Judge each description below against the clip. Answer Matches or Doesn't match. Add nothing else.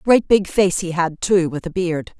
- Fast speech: Matches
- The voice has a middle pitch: Matches